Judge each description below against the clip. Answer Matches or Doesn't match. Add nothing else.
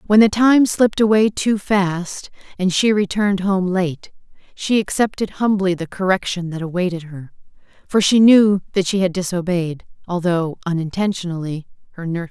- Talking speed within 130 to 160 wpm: Matches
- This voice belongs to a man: Doesn't match